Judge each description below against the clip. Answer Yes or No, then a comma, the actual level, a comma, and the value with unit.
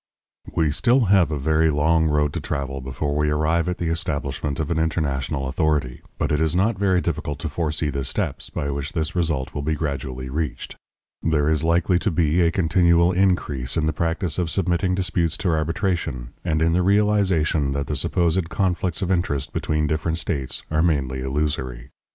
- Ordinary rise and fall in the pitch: Yes, average, 3.1 semitones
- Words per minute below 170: No, average, 185 wpm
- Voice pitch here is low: Yes, very low, 80 Hz